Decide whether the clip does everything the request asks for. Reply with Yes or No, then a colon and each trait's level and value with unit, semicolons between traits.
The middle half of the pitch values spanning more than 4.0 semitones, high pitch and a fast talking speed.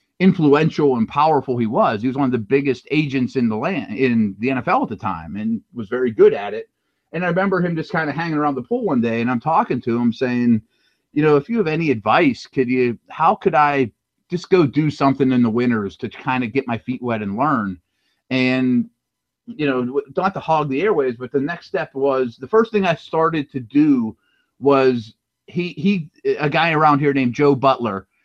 No: wide, 5.5 semitones; medium, 140 Hz; fast, 220 wpm